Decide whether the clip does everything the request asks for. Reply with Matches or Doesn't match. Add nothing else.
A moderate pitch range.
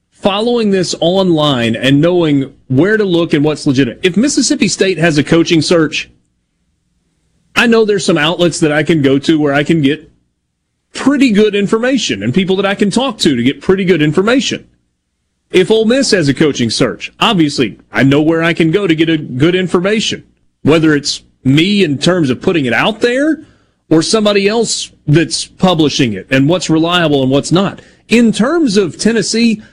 Doesn't match